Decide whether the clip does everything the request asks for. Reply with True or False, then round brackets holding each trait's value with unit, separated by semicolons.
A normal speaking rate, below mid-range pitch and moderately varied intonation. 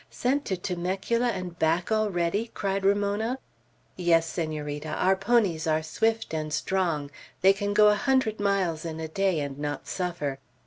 False (160 wpm; 185 Hz; 4.3 semitones)